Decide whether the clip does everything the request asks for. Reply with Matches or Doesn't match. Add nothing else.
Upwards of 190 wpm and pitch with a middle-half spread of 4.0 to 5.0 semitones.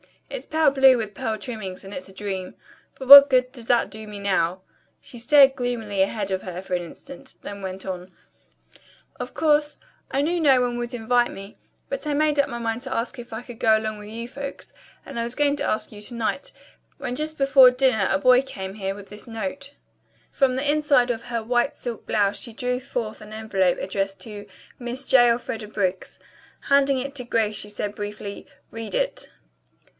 Matches